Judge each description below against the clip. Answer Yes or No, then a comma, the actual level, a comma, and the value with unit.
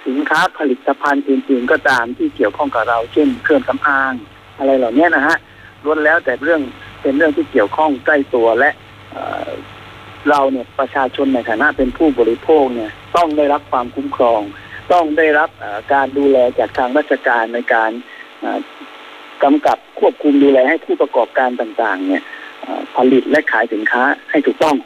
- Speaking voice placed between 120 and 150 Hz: Yes, low, 135 Hz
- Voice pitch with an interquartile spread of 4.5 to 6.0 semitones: No, average, 4.1 semitones